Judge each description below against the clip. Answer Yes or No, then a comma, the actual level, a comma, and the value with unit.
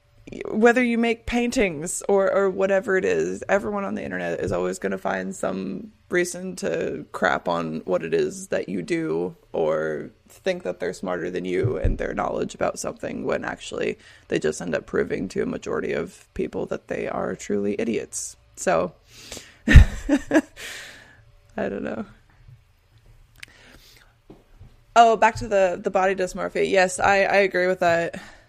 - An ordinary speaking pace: Yes, average, 160 wpm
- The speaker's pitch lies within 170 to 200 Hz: Yes, medium, 185 Hz